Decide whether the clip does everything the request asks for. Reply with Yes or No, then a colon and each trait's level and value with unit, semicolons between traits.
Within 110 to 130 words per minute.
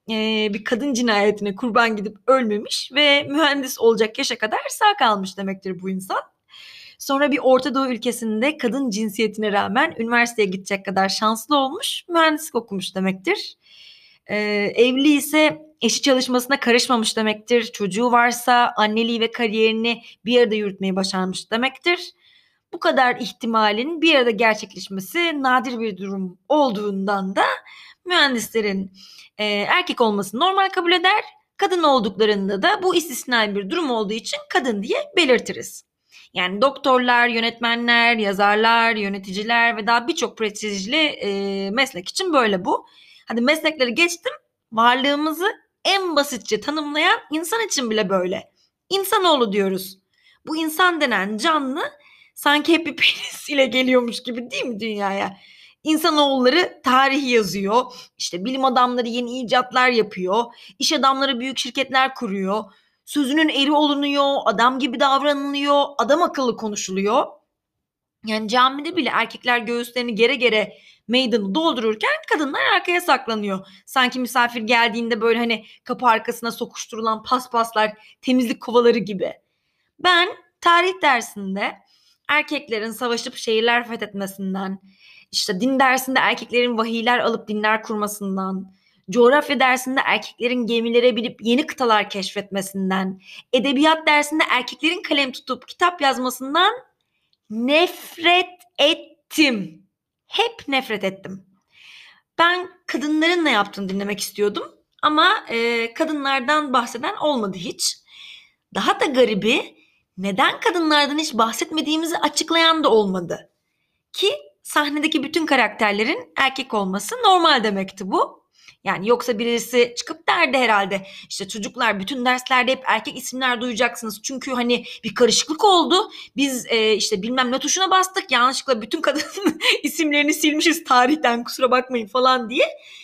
Yes: average, 120 wpm